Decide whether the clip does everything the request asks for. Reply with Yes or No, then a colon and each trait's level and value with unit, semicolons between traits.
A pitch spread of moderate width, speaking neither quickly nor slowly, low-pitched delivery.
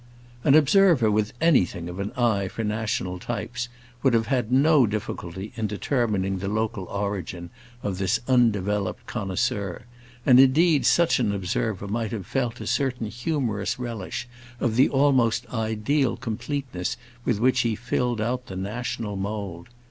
Yes: average, 4.0 semitones; average, 150 wpm; low, 110 Hz